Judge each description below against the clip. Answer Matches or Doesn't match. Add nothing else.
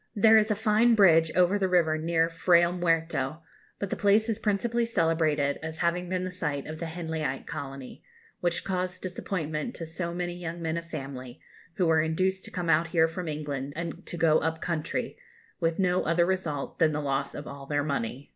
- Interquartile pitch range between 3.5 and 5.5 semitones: Doesn't match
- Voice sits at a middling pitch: Matches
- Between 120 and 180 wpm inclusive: Doesn't match